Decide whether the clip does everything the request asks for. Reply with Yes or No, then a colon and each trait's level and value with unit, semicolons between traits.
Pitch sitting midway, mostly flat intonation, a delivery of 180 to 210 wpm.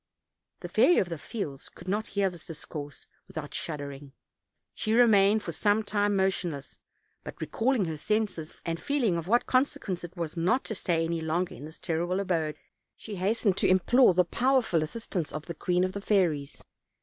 No: medium, 180 Hz; average, 4.6 semitones; average, 185 wpm